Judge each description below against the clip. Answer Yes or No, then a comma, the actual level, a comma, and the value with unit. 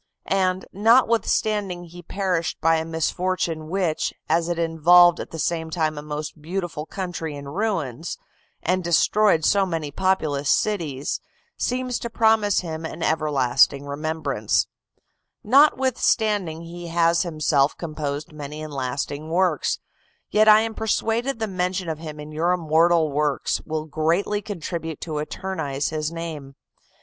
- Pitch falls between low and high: Yes, medium, 165 Hz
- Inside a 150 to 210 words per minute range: No, average, 140 wpm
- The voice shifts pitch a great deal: No, average, 3.7 semitones